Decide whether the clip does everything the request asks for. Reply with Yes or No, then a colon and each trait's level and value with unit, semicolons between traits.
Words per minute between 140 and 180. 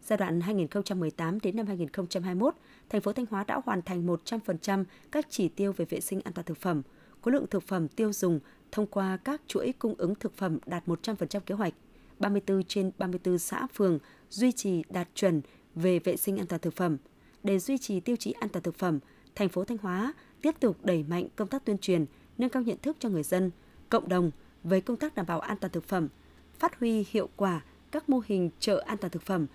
No: average, 220 wpm